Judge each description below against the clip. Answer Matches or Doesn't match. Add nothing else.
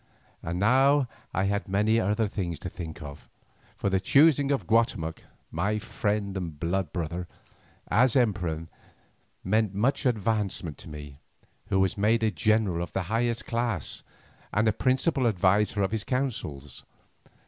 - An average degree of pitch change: Matches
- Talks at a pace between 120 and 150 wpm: Matches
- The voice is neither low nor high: Doesn't match